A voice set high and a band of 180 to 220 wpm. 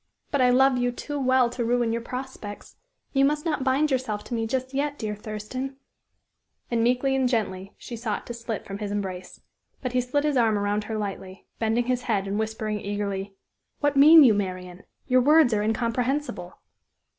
Yes: high, 235 Hz; average, 190 wpm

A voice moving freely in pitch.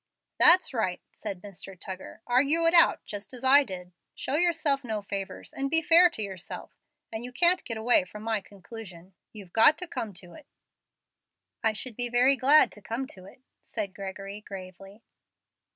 Yes: wide, 5.8 semitones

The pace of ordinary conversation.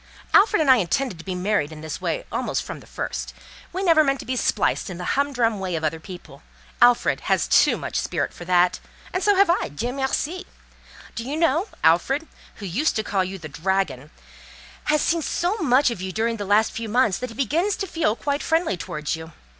No: fast, 215 wpm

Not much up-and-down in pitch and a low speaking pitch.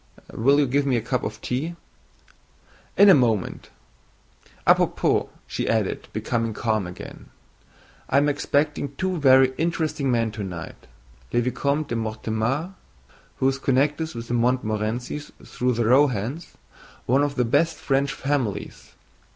No: average, 3.9 semitones; low, 130 Hz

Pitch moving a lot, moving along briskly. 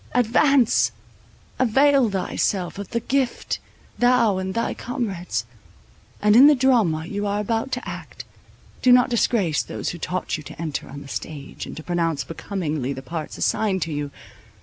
No: wide, 6.9 semitones; average, 165 wpm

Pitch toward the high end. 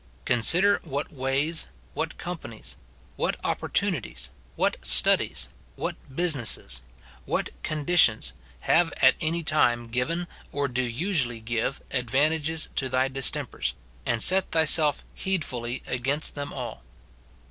No: medium, 140 Hz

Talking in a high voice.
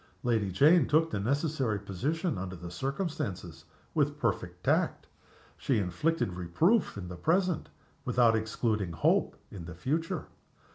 No: low, 115 Hz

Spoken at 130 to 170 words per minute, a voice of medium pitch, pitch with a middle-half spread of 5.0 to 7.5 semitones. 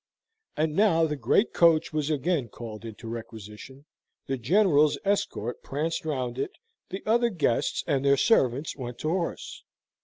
Yes: average, 150 wpm; medium, 145 Hz; average, 5.3 semitones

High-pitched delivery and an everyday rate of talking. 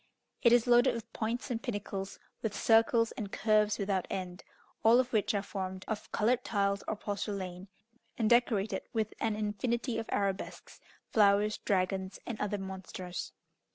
Yes: high, 210 Hz; average, 155 wpm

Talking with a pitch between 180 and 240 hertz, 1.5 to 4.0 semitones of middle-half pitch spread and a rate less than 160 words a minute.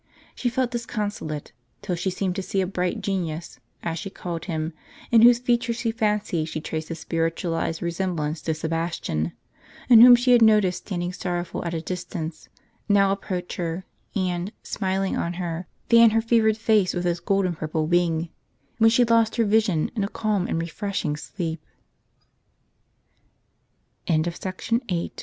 No: medium, 185 Hz; average, 4.5 semitones; average, 150 wpm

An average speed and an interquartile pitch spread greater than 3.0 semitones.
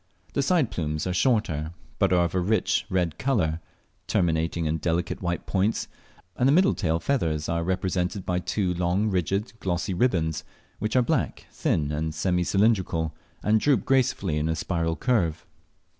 Yes: average, 165 wpm; average, 4.6 semitones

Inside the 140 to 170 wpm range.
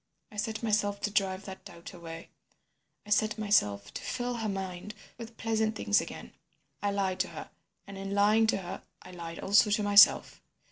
No: average, 180 wpm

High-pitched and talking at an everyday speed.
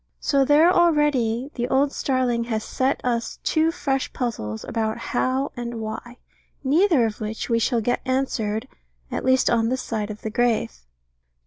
Yes: high, 245 Hz; average, 160 wpm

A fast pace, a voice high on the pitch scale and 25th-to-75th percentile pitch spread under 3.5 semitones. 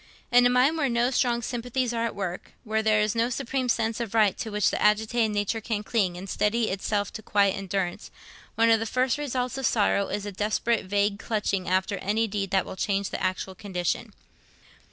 Yes: fast, 210 wpm; high, 215 Hz; average, 2.9 semitones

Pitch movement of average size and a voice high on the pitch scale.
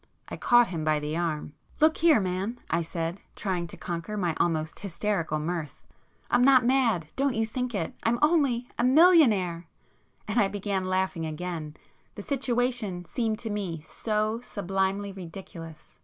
No: wide, 6.1 semitones; high, 195 Hz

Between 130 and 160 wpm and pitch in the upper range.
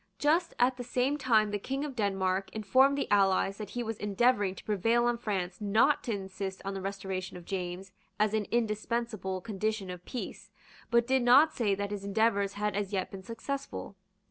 No: average, 195 wpm; high, 210 Hz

